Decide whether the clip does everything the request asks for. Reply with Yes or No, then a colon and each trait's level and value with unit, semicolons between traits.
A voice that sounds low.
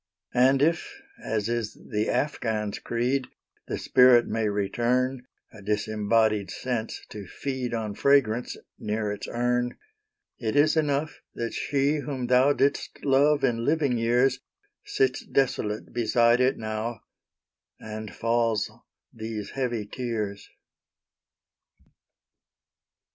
Yes: low, 120 Hz